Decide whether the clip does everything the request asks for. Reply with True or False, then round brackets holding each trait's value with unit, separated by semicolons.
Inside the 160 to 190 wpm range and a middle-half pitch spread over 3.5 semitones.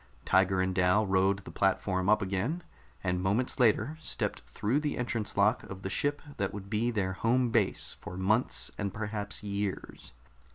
False (170 wpm; 3.0 semitones)